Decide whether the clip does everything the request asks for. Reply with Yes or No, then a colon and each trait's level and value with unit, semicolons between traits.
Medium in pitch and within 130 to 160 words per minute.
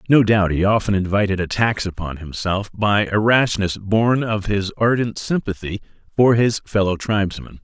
No: low, 105 Hz; average, 155 wpm